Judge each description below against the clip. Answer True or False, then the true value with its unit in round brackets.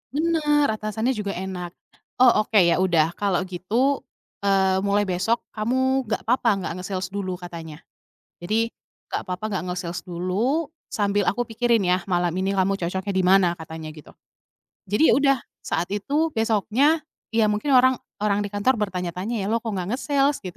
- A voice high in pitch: True (200 Hz)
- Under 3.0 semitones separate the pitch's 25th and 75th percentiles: False (4.3 semitones)